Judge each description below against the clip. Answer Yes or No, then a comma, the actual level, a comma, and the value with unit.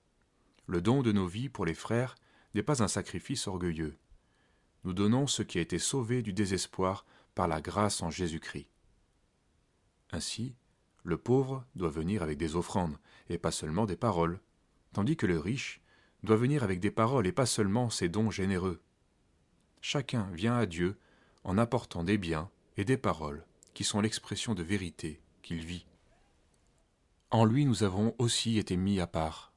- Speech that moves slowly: No, average, 165 wpm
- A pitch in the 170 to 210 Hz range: No, low, 100 Hz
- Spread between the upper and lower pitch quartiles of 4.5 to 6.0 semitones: Yes, average, 4.9 semitones